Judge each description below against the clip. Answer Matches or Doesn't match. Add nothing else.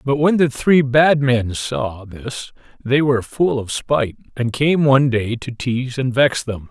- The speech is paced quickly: Doesn't match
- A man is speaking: Matches